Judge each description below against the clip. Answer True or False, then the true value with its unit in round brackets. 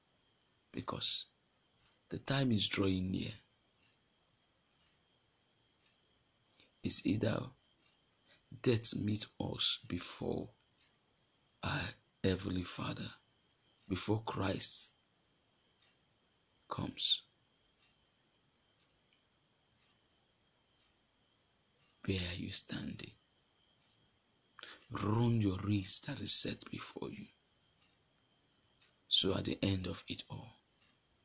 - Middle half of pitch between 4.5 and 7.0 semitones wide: False (3.4 semitones)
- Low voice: True (105 Hz)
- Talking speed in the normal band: False (70 wpm)